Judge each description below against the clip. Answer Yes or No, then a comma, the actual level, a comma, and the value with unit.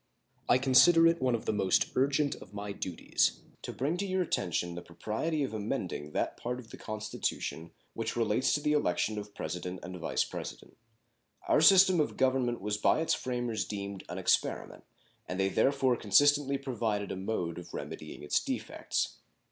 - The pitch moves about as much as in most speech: No, wide, 5.9 semitones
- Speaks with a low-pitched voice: Yes, low, 115 Hz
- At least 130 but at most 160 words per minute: No, average, 175 wpm